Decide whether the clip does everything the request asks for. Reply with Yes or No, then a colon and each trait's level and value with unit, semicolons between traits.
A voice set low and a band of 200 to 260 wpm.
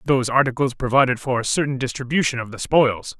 No: low, 130 Hz; average, 190 wpm